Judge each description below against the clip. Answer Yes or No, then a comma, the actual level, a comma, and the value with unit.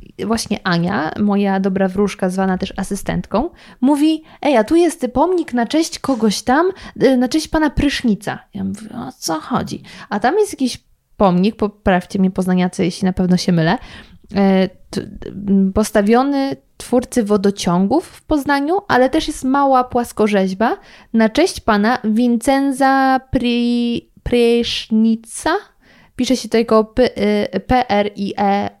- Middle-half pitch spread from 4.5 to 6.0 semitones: Yes, average, 5.1 semitones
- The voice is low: No, high, 225 Hz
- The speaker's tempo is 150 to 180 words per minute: No, average, 130 wpm